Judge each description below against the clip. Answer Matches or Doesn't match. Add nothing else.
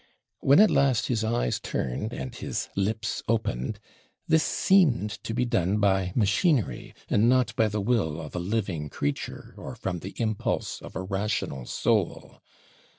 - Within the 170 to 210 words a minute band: Doesn't match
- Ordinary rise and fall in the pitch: Matches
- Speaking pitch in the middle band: Doesn't match